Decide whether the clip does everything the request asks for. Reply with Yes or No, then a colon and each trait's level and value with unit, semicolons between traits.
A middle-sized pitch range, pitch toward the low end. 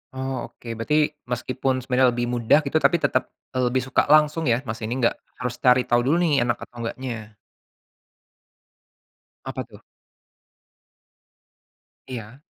No: narrow, 2.0 semitones; low, 125 Hz